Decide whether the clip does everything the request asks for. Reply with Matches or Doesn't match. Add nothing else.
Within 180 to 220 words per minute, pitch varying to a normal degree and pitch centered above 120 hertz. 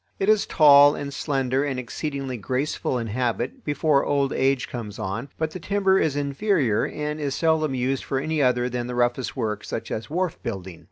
Matches